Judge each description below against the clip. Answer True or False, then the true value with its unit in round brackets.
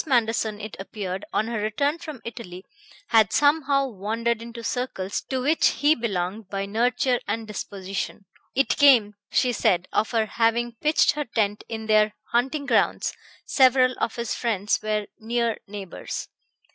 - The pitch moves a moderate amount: True (3.3 semitones)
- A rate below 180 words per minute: True (150 wpm)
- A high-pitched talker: True (225 Hz)